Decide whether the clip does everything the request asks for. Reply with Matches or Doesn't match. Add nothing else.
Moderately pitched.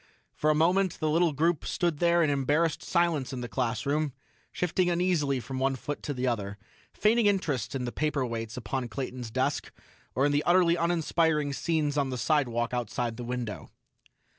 Matches